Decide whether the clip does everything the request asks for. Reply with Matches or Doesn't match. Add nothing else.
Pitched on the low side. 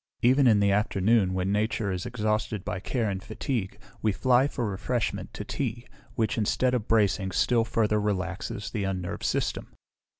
Matches